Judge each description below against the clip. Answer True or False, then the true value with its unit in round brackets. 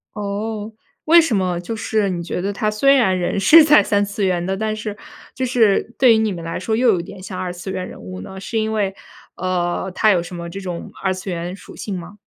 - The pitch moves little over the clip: False (3.3 semitones)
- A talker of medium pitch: False (195 Hz)